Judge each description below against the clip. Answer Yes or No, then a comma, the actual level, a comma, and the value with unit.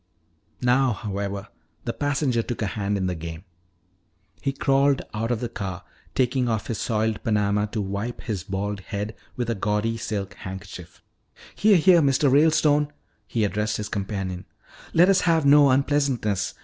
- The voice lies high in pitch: No, low, 110 Hz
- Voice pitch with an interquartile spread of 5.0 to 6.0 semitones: Yes, average, 5.3 semitones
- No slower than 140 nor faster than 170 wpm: Yes, average, 160 wpm